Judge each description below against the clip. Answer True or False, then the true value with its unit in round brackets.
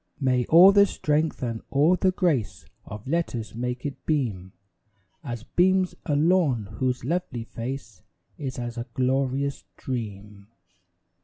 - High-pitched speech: False (130 Hz)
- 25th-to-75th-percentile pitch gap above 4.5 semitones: True (5.0 semitones)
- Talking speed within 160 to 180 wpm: False (135 wpm)